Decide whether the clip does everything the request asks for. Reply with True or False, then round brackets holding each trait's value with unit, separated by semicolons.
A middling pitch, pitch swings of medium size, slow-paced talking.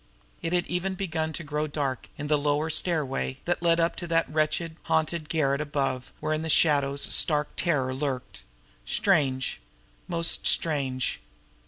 False (155 Hz; 3.0 semitones; 160 wpm)